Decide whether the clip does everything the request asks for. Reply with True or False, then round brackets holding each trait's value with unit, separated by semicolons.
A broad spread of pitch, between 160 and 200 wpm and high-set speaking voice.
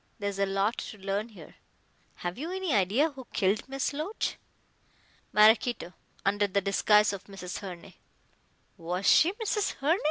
False (5.7 semitones; 150 wpm; 205 Hz)